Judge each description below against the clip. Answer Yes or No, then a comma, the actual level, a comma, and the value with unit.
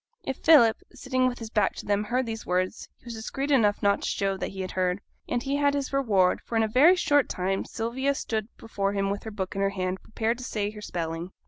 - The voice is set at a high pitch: Yes, high, 220 Hz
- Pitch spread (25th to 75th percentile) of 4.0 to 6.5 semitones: Yes, average, 4.5 semitones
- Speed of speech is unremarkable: No, fast, 245 wpm